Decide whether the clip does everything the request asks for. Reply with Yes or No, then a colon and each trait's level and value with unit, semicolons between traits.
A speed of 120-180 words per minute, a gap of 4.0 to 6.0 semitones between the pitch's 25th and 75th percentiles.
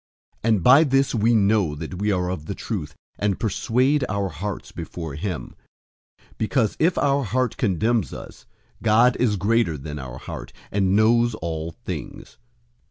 Yes: average, 165 wpm; average, 5.1 semitones